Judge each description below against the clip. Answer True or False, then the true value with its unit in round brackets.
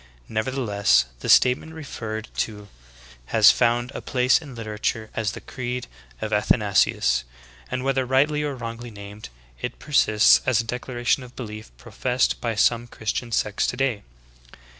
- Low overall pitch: True (120 Hz)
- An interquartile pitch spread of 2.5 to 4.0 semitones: True (2.9 semitones)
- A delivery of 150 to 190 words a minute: False (140 wpm)